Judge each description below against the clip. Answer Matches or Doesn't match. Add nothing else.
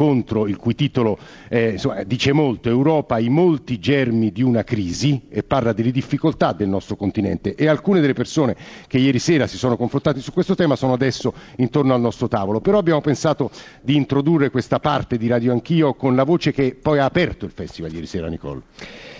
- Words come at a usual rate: Doesn't match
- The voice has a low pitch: Matches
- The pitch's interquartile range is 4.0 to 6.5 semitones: Matches